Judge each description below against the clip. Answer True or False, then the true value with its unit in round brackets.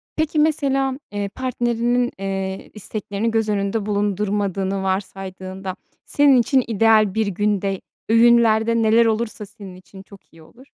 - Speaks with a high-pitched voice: True (210 Hz)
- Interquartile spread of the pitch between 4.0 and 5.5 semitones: False (3.2 semitones)